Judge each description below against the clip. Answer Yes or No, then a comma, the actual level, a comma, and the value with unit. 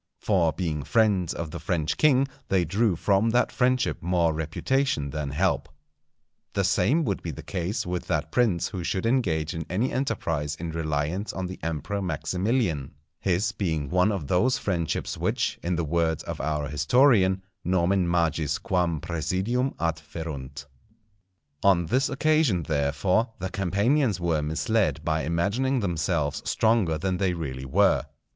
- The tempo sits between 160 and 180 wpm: No, average, 150 wpm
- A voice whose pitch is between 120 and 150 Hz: No, very low, 90 Hz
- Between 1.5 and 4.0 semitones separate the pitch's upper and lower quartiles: No, average, 4.5 semitones